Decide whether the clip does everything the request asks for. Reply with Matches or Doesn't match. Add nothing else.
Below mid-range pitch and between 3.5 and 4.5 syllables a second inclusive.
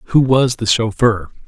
Matches